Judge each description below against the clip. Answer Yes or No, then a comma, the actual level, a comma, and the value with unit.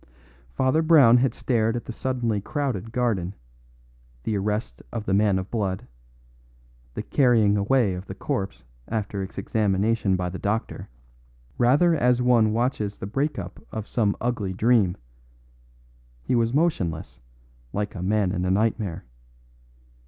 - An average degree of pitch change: Yes, average, 4.0 semitones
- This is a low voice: Yes, low, 110 Hz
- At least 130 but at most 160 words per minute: Yes, average, 145 wpm